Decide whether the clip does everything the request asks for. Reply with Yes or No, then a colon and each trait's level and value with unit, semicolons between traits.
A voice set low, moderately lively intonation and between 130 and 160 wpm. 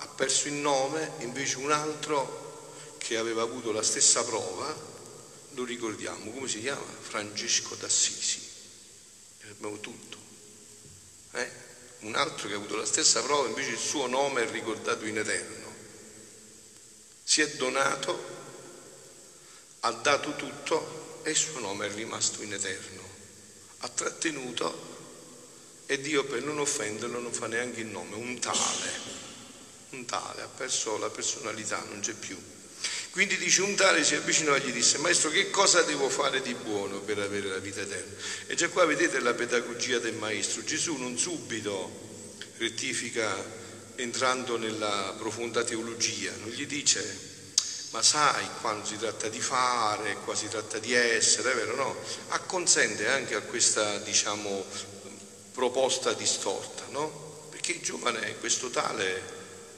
No: low, 115 Hz; wide, 6.0 semitones; average, 145 wpm